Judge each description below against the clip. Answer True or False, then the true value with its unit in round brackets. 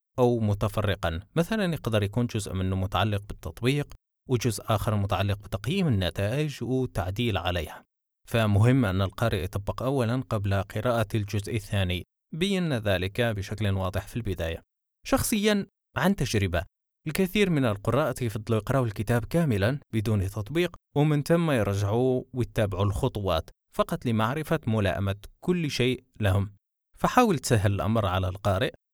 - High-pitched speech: False (110 Hz)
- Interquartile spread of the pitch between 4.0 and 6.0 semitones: True (4.8 semitones)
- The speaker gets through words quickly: False (120 wpm)